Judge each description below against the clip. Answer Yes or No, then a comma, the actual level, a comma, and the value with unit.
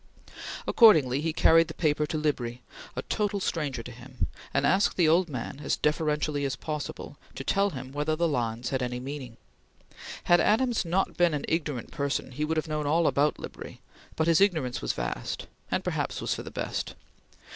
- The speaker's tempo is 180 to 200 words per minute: Yes, average, 190 wpm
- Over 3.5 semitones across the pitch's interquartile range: Yes, average, 4.1 semitones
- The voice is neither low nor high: Yes, medium, 150 Hz